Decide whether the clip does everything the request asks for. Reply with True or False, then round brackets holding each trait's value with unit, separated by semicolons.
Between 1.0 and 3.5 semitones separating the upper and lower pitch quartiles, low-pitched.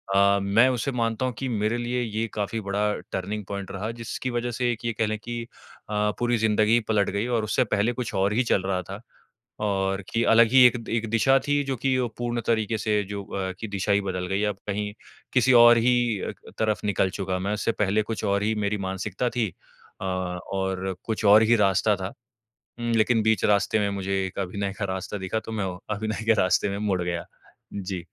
True (2.9 semitones; 105 Hz)